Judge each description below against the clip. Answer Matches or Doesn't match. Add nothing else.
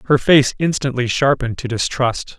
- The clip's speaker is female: Doesn't match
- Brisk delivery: Doesn't match